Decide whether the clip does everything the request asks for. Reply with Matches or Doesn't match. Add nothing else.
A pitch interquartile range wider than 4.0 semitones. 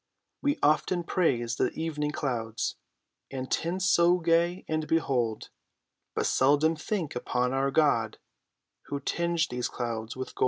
Matches